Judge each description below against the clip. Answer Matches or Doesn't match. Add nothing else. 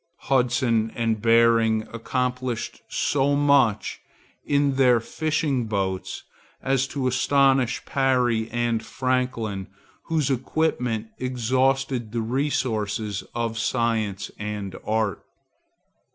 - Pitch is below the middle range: Matches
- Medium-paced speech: Doesn't match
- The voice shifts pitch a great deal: Doesn't match